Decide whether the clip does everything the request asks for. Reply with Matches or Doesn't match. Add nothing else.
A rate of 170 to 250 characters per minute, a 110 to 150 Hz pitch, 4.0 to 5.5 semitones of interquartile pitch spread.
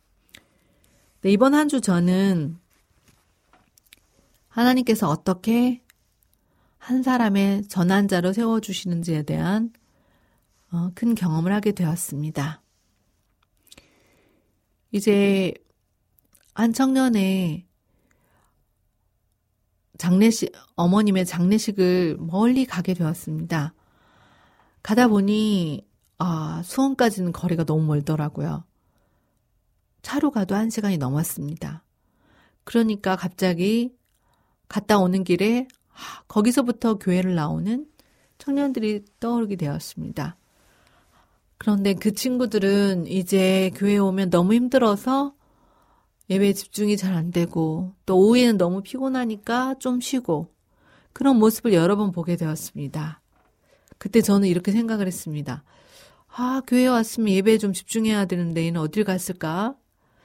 Doesn't match